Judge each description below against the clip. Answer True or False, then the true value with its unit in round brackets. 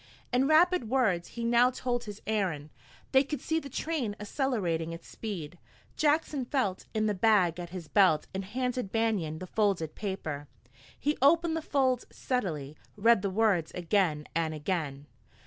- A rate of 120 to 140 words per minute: False (160 wpm)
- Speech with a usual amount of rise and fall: False (6.8 semitones)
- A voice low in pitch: False (210 Hz)